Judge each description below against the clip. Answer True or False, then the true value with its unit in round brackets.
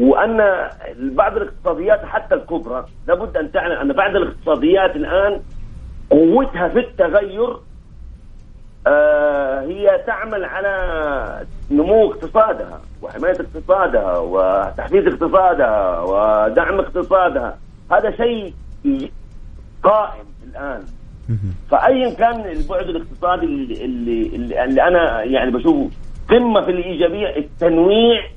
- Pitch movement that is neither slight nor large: False (6.7 semitones)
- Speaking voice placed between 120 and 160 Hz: False (190 Hz)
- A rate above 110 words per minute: False (95 wpm)